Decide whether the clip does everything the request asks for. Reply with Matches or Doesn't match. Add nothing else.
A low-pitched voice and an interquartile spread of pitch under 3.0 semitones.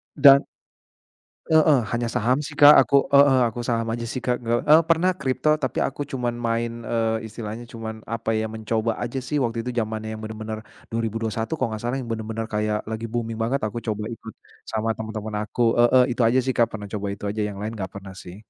Matches